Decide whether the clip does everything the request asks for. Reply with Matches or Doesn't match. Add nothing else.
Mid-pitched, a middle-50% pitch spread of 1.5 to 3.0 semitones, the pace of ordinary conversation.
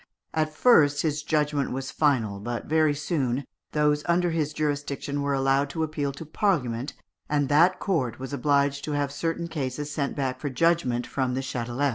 Matches